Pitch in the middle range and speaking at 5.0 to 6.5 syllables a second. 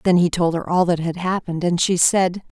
Yes: medium, 175 Hz; 5.5 syllables/s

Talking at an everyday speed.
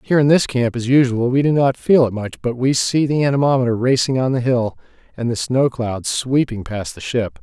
No: fast, 235 wpm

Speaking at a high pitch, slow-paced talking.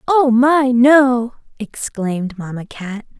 Yes: high, 240 Hz; slow, 115 wpm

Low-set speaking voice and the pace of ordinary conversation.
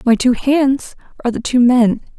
No: very high, 250 Hz; average, 190 wpm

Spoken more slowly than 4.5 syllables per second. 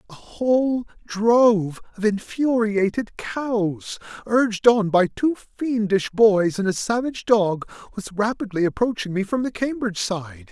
Yes: 4.3 syllables/s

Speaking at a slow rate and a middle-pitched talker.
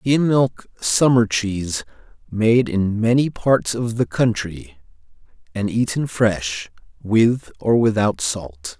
No: slow, 125 wpm; low, 110 Hz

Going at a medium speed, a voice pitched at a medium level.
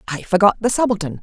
No: average, 195 wpm; high, 195 Hz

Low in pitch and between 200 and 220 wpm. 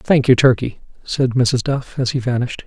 Yes: low, 125 Hz; fast, 205 wpm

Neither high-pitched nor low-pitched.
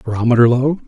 No: low, 125 Hz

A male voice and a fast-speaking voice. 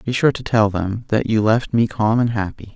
Yes: male; fast, 260 wpm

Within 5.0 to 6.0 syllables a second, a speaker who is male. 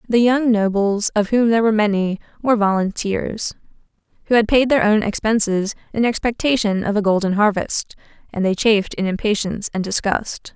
No: 5.4 syllables/s; female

